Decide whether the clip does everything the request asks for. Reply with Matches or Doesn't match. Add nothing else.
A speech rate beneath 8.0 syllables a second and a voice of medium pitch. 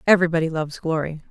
Doesn't match